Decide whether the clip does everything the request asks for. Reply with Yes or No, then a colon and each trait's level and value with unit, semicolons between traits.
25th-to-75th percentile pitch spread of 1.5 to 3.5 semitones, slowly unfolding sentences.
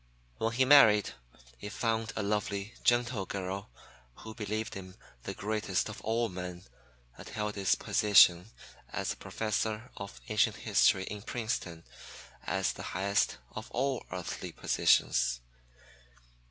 Yes: average, 2.8 semitones; slow, 125 wpm